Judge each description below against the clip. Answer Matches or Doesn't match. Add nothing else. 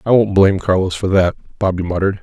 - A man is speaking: Matches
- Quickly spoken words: Matches